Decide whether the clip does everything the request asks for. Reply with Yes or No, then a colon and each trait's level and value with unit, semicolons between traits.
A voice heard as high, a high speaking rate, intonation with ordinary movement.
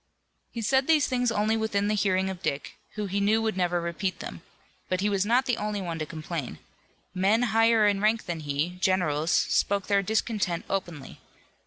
No: high, 200 Hz; average, 190 wpm; average, 3.7 semitones